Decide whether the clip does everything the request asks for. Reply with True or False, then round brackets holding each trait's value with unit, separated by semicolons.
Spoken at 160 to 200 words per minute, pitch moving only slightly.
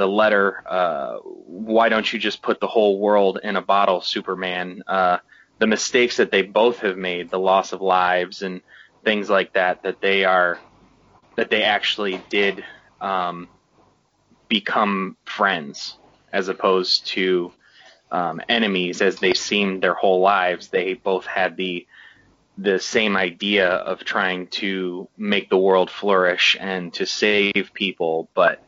False (150 wpm; 1.9 semitones)